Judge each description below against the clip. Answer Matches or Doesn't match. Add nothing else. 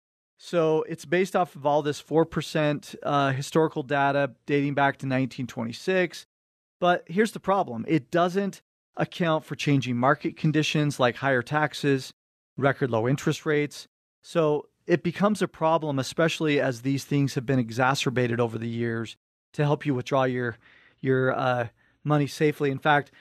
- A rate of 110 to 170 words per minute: Matches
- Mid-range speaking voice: Matches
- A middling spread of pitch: Matches